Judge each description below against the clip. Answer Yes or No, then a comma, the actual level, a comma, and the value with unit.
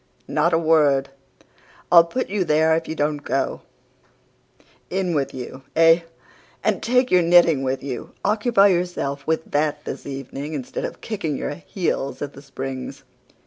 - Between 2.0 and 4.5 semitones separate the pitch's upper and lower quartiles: Yes, average, 4.0 semitones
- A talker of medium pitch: Yes, medium, 155 Hz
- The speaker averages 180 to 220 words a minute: No, average, 160 wpm